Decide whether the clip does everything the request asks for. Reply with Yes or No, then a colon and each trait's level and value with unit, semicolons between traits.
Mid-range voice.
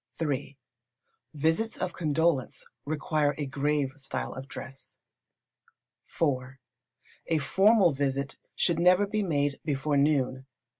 Yes: medium, 145 Hz